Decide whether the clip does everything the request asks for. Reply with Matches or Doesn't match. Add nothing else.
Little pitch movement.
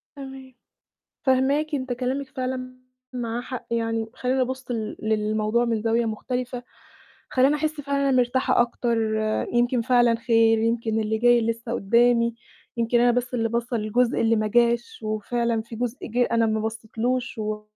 Matches